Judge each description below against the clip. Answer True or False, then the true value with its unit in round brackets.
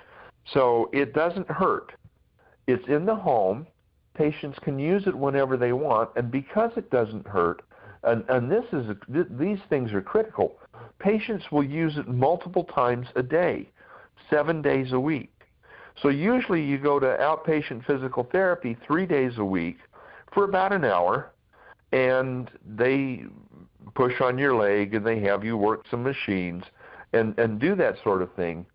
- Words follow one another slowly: False (165 wpm)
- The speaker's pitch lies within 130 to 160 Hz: True (135 Hz)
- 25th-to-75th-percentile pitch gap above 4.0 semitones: True (5.5 semitones)